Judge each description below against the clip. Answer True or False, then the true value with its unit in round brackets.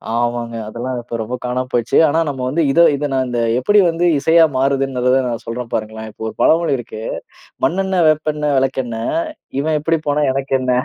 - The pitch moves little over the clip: False (4.0 semitones)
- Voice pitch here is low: True (130 Hz)